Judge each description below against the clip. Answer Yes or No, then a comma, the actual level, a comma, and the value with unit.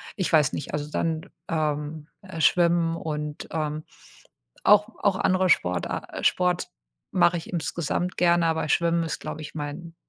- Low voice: No, medium, 165 Hz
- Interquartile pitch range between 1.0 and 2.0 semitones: No, narrow, 2.4 semitones